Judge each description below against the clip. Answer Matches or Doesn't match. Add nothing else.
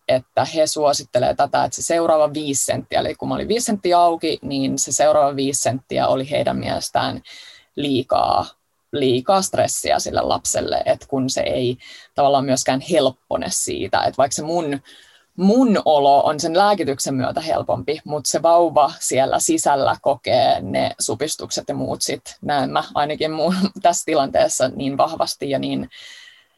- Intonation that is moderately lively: Doesn't match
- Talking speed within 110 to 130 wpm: Doesn't match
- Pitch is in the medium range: Matches